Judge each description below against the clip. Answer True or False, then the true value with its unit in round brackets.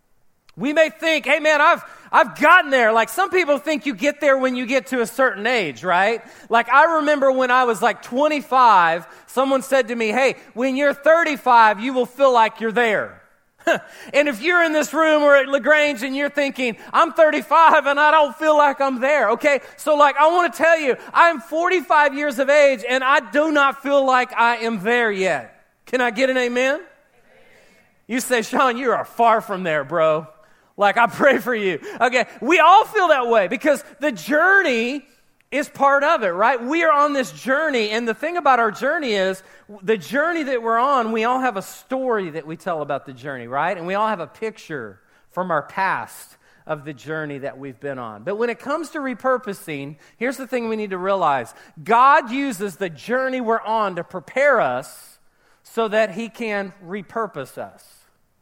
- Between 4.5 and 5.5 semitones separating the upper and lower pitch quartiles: True (5.0 semitones)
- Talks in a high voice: True (255 Hz)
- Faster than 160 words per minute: True (200 wpm)